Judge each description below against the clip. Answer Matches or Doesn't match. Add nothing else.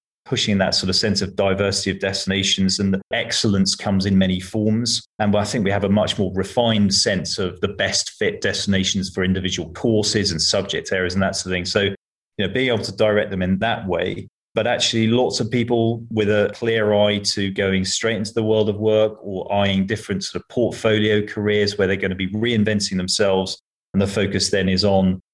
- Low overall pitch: Matches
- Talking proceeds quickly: Matches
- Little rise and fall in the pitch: Matches